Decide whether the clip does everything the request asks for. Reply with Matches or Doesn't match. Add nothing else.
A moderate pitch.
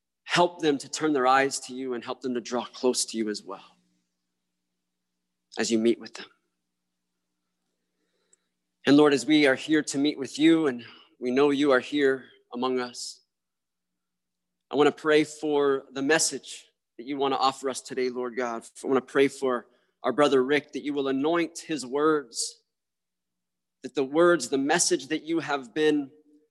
Doesn't match